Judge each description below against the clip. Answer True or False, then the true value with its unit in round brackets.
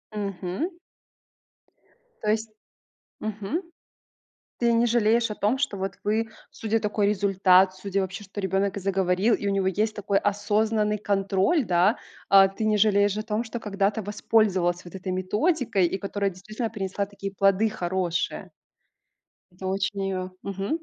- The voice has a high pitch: True (200 Hz)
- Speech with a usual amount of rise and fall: False (2.1 semitones)